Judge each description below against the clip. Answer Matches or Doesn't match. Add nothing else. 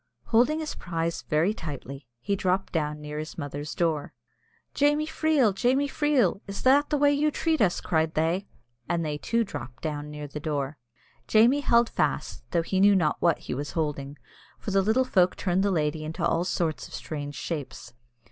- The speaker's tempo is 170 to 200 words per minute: Matches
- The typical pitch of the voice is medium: Matches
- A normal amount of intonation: Doesn't match